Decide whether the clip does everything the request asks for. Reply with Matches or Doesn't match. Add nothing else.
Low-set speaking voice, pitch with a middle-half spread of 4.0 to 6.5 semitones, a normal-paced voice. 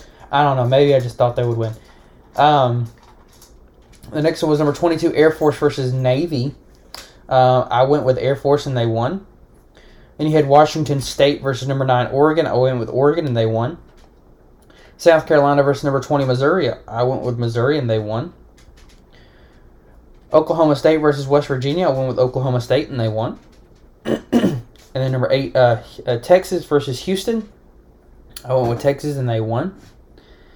Matches